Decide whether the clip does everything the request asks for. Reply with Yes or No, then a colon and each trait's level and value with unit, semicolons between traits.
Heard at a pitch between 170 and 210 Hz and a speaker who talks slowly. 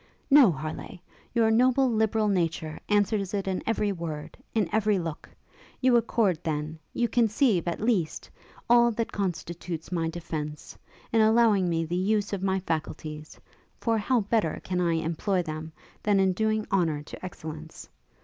No: high, 190 Hz; average, 155 wpm